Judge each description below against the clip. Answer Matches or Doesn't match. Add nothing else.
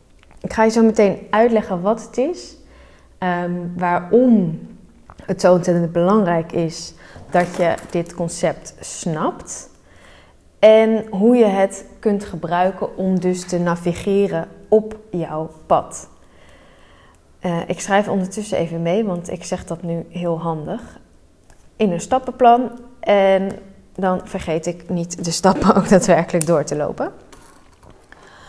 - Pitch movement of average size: Matches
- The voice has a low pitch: Doesn't match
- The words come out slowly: Matches